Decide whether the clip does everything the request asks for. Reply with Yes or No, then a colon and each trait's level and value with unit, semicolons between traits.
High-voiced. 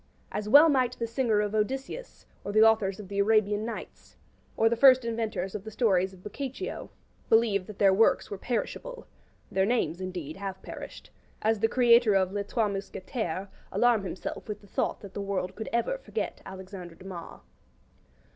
Yes: high, 210 Hz